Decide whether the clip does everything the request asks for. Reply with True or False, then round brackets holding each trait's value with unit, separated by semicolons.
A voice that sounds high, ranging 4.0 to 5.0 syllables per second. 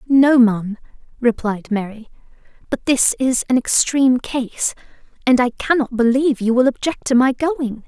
True (250 Hz; 4.8 syllables/s)